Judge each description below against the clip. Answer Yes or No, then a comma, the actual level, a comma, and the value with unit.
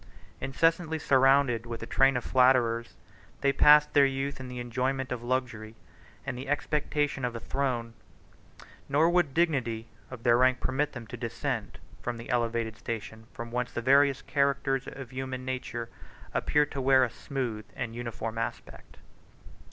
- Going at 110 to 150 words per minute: No, average, 160 wpm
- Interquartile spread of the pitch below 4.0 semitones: Yes, average, 2.8 semitones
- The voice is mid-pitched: No, low, 130 Hz